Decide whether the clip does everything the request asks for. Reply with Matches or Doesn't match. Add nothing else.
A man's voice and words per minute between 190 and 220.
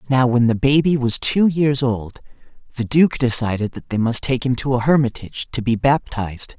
Matches